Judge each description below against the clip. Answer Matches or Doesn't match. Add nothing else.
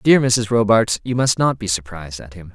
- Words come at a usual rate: Doesn't match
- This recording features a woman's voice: Doesn't match